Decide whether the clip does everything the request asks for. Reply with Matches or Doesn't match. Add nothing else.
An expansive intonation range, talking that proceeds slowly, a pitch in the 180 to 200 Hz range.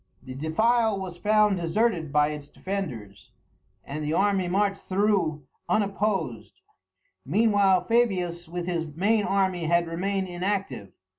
Doesn't match